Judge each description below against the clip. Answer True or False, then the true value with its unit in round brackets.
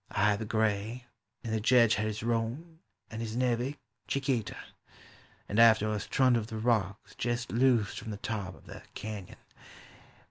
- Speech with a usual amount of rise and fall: False (2.1 semitones)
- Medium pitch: False (110 Hz)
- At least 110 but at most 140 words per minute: False (170 wpm)